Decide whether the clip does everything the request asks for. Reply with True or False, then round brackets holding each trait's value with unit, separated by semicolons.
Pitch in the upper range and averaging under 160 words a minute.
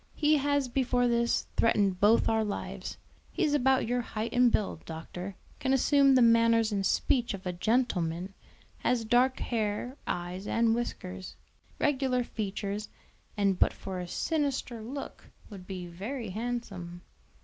True (230 Hz; 150 wpm)